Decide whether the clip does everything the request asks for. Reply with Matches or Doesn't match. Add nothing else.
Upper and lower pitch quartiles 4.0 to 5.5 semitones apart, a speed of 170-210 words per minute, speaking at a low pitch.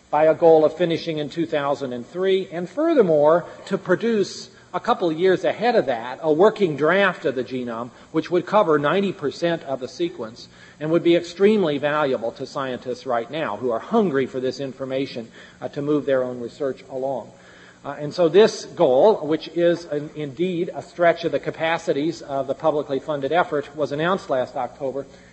Doesn't match